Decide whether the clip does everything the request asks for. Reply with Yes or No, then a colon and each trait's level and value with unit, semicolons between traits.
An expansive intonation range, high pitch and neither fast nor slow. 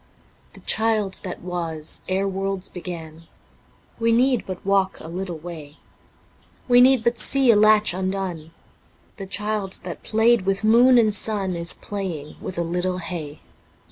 No: average, 3.7 semitones; high, 195 Hz; average, 160 wpm